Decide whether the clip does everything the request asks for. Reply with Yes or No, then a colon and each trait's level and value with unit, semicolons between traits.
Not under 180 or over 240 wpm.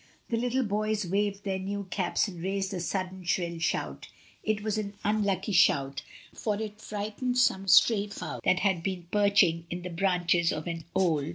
Yes: average, 195 wpm